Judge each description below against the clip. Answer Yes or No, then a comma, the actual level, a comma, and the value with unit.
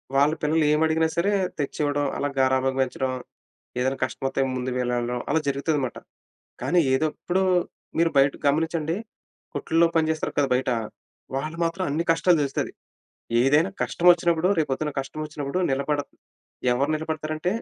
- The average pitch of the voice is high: No, medium, 150 Hz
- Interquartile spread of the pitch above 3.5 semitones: No, average, 3.2 semitones